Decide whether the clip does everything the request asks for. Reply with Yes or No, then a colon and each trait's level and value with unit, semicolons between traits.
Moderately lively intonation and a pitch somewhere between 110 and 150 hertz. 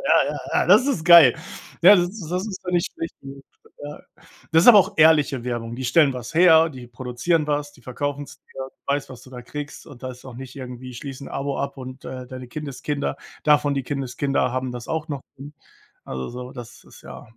Yes: average, 3.4 semitones; medium, 140 Hz